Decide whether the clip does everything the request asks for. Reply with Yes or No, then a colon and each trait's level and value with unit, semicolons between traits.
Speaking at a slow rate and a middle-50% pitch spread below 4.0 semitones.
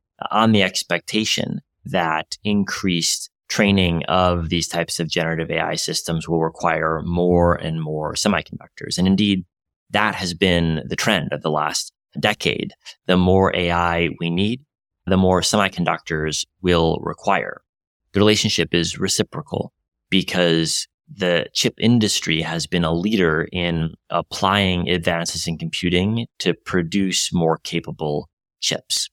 Yes: slow, 130 wpm; narrow, 2.6 semitones